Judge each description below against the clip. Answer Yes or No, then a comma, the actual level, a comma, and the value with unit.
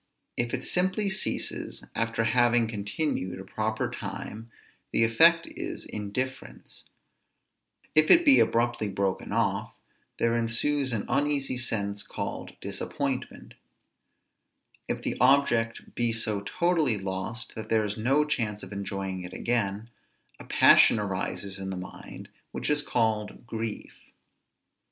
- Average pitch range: Yes, average, 4.1 semitones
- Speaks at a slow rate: Yes, slow, 130 wpm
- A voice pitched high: No, low, 115 Hz